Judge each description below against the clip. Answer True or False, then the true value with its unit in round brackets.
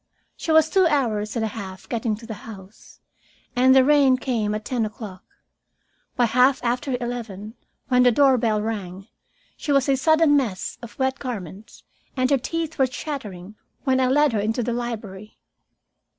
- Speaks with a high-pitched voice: True (240 Hz)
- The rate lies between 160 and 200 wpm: True (170 wpm)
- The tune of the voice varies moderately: True (3.9 semitones)